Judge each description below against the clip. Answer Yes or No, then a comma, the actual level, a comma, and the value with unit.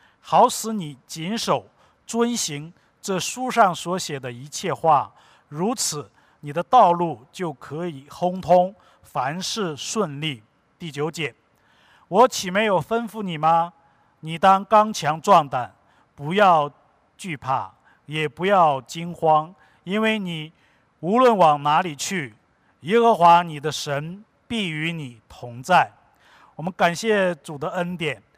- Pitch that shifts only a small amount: No, average, 4.7 semitones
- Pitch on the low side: No, medium, 170 Hz